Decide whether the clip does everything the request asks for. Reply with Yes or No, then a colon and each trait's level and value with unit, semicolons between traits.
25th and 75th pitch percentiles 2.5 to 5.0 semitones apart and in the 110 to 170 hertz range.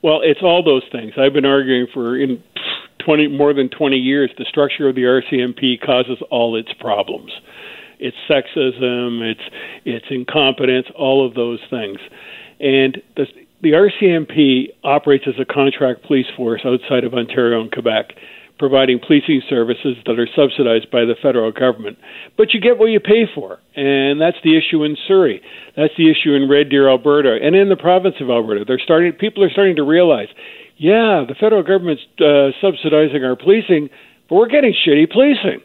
No: wide, 5.5 semitones; medium, 140 Hz